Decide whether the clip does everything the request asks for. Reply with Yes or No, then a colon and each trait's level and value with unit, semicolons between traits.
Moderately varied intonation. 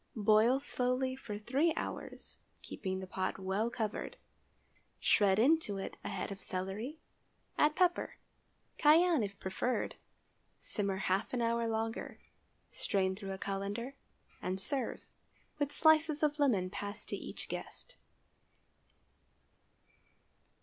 No: wide, 6.0 semitones